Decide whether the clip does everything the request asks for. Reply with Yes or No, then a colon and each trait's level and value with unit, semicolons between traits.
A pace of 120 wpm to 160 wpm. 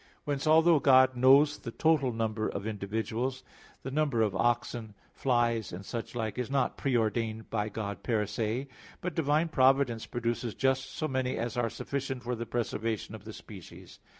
No: average, 175 wpm